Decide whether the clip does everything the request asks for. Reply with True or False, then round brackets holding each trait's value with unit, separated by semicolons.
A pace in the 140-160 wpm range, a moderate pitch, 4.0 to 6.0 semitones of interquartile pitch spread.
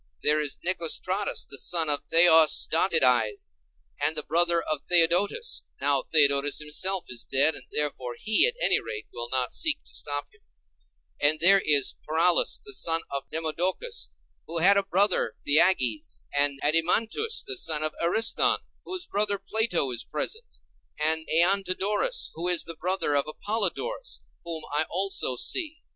True (150 wpm; 170 Hz; 5.2 semitones)